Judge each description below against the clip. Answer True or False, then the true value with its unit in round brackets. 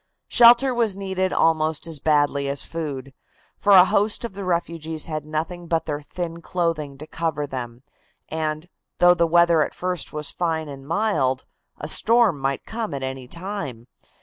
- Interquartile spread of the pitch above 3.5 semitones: True (3.9 semitones)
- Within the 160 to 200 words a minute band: True (170 wpm)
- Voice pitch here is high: False (160 Hz)